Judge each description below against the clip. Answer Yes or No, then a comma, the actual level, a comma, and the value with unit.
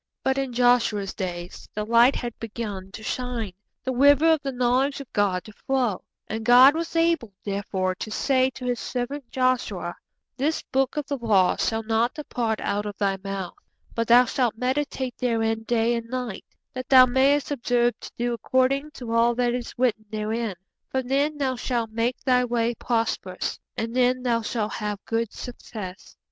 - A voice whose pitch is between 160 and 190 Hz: No, high, 240 Hz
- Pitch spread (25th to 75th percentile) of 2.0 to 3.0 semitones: Yes, average, 2.7 semitones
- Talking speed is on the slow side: No, average, 180 wpm